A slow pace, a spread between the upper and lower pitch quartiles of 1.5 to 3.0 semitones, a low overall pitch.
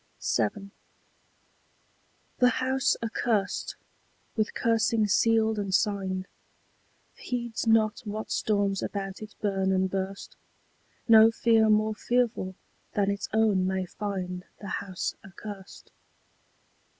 No: slow, 105 wpm; narrow, 2.4 semitones; high, 210 Hz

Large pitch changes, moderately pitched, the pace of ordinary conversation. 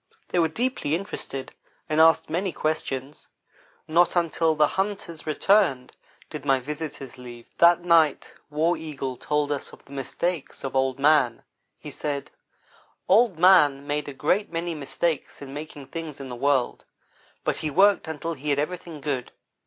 No: average, 3.4 semitones; medium, 150 Hz; average, 160 wpm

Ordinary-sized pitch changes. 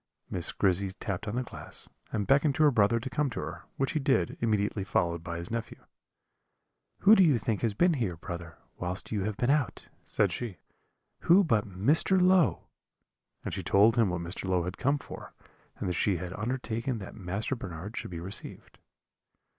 No: wide, 6.3 semitones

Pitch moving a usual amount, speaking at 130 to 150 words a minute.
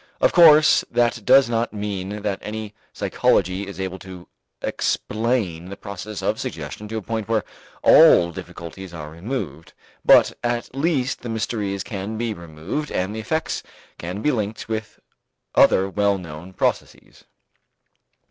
Yes: average, 3.5 semitones; average, 145 wpm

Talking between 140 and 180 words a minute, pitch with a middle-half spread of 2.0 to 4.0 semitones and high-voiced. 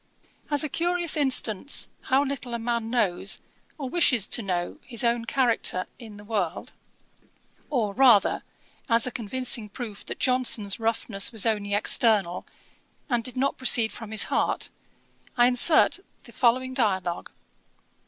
Yes: average, 145 wpm; average, 3.7 semitones; high, 235 Hz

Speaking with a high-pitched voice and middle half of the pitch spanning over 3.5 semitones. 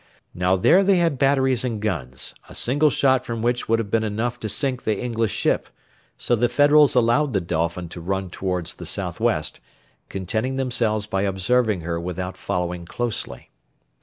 No: low, 110 Hz; wide, 5.4 semitones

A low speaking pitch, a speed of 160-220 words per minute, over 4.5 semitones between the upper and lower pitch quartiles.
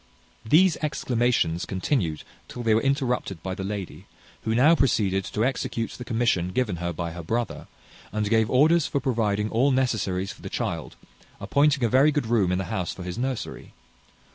Yes: low, 115 Hz; average, 180 wpm; wide, 5.4 semitones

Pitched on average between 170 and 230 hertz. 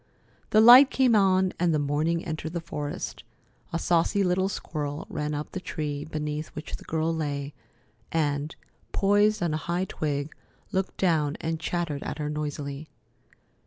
No: medium, 160 Hz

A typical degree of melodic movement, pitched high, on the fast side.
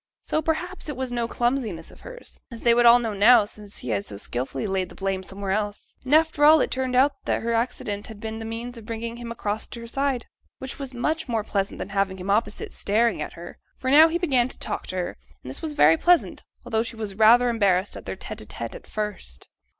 Yes: average, 4.2 semitones; high, 230 Hz; fast, 245 wpm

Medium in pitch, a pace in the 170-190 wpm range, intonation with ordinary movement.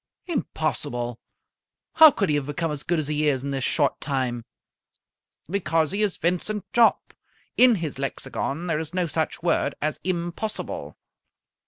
No: medium, 160 Hz; average, 155 wpm; average, 4.2 semitones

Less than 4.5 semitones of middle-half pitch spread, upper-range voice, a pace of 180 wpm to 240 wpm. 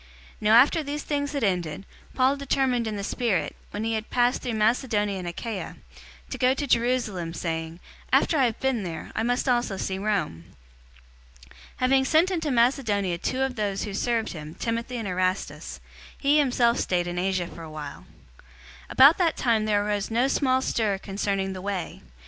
No: average, 5.0 semitones; high, 220 Hz; average, 185 wpm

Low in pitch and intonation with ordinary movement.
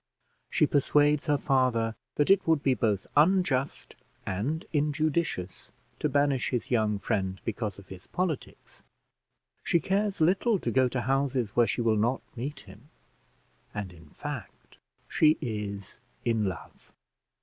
No: low, 130 Hz; wide, 5.9 semitones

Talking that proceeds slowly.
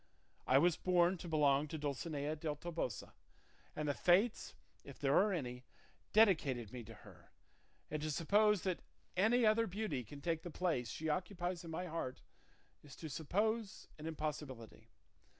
No: average, 160 wpm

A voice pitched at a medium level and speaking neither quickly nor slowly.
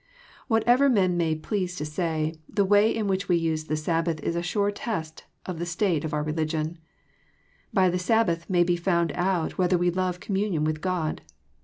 Yes: medium, 175 Hz; average, 190 wpm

